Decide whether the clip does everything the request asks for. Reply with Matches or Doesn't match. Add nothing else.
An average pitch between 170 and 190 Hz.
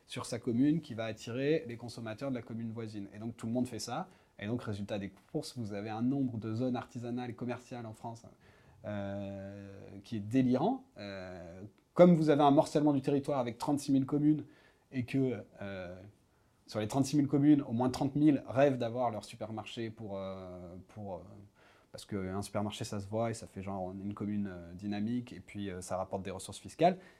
Doesn't match